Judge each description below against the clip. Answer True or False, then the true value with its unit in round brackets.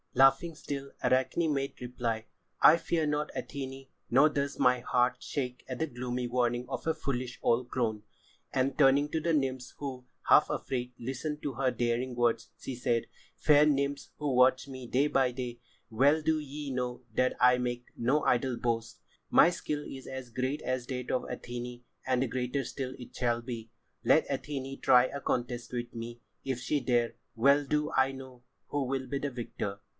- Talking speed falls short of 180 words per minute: False (185 wpm)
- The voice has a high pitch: False (130 Hz)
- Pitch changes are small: True (2.2 semitones)